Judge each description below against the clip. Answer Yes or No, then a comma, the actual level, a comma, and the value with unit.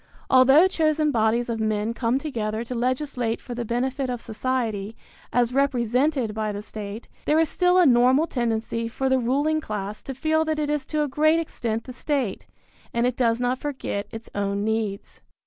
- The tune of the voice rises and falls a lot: No, average, 4.2 semitones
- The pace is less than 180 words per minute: No, average, 185 wpm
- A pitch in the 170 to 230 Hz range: No, high, 245 Hz